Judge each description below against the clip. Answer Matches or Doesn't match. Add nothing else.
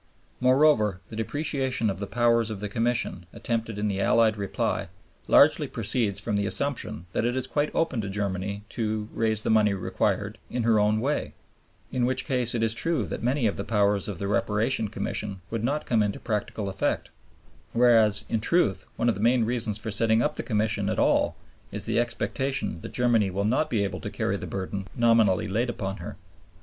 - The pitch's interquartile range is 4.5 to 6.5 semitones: Doesn't match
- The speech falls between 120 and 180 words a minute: Doesn't match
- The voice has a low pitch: Matches